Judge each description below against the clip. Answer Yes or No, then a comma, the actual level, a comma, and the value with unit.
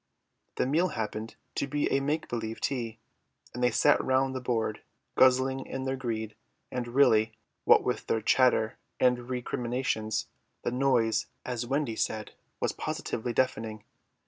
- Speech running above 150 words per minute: No, average, 145 wpm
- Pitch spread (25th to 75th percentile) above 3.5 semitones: No, average, 2.9 semitones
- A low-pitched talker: Yes, low, 125 Hz